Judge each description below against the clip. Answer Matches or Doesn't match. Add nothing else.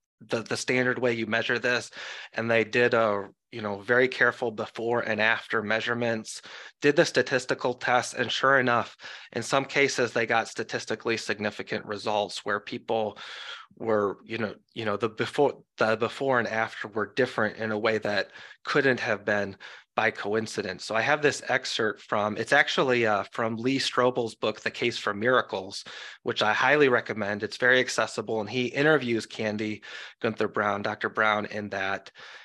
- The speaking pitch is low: Matches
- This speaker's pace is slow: Doesn't match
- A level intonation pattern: Matches